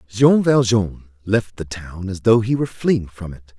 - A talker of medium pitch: No, low, 105 Hz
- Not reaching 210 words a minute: Yes, average, 200 wpm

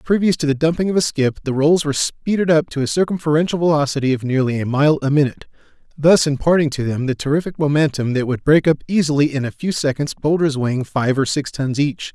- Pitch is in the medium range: Yes, medium, 145 Hz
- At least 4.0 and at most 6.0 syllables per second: No, 6.3 syllables/s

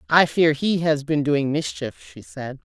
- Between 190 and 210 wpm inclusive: Yes, average, 200 wpm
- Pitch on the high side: No, medium, 150 Hz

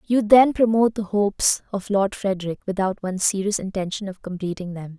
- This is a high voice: Yes, high, 200 Hz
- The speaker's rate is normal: Yes, average, 180 wpm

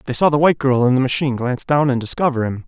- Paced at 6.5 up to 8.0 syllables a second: Yes, 7.6 syllables/s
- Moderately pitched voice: No, low, 130 Hz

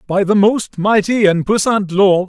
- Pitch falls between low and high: No, high, 200 Hz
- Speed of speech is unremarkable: Yes, average, 185 wpm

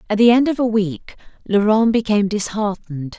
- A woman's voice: Yes, female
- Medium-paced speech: Yes, average, 170 wpm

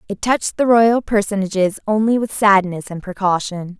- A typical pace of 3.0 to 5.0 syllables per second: No, 5.2 syllables/s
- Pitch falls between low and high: No, high, 205 Hz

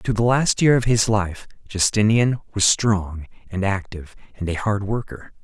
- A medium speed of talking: Yes, average, 175 wpm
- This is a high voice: No, low, 105 Hz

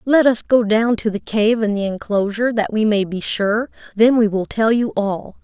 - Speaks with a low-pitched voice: No, high, 220 Hz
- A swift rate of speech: Yes, fast, 230 wpm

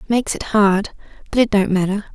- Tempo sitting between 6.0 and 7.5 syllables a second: No, 5.7 syllables/s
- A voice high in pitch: Yes, high, 205 Hz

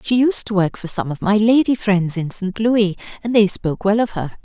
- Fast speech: Yes, fast, 255 wpm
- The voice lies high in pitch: Yes, high, 205 Hz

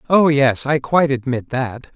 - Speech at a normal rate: Yes, average, 185 wpm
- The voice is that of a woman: No, male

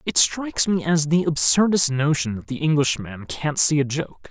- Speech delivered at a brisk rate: No, average, 195 wpm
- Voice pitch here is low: No, medium, 150 Hz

